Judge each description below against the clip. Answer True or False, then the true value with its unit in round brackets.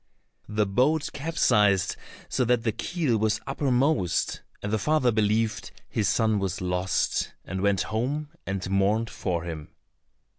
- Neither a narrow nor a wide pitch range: True (4.4 semitones)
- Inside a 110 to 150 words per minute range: True (140 wpm)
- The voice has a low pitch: True (110 Hz)